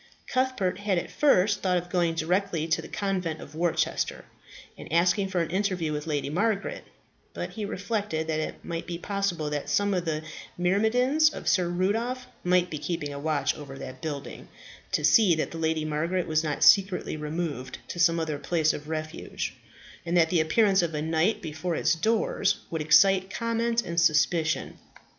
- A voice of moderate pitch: Yes, medium, 175 Hz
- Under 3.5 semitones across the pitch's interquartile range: No, average, 3.9 semitones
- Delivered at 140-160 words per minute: No, average, 180 wpm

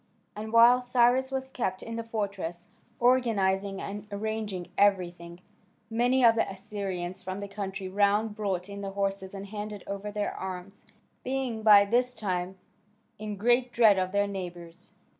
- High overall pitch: Yes, high, 205 Hz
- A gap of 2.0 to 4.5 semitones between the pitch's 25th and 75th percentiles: Yes, average, 3.0 semitones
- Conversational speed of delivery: Yes, average, 155 wpm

